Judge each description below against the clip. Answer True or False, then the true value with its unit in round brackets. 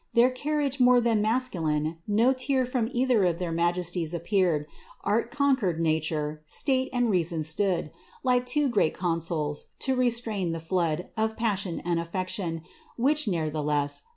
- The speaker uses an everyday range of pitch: False (7.0 semitones)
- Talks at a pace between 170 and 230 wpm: False (145 wpm)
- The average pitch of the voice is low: False (190 Hz)